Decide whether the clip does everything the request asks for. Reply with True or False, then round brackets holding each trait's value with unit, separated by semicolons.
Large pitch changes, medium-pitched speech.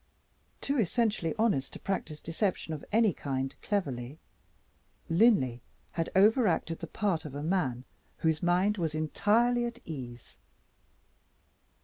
True (6.0 semitones; 170 Hz)